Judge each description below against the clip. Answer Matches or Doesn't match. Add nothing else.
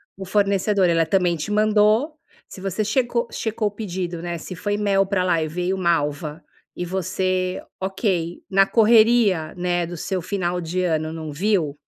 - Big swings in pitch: Doesn't match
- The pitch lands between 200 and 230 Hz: Doesn't match